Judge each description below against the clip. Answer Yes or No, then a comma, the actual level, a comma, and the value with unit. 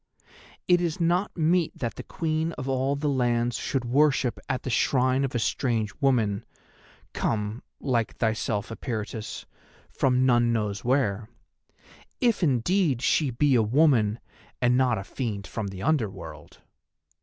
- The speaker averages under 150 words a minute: Yes, average, 140 wpm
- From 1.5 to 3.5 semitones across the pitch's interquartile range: No, average, 4.1 semitones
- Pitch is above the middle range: No, low, 125 Hz